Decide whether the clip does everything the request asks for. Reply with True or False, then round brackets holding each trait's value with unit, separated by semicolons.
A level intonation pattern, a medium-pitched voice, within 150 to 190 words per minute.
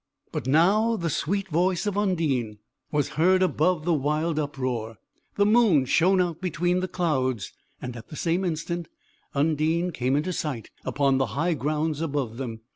False (4.6 semitones; 155 Hz; 165 wpm)